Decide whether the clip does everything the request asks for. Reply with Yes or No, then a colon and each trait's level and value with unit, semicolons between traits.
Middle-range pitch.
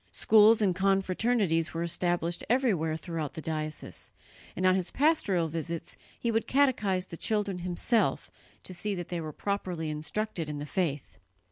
Yes: medium, 180 Hz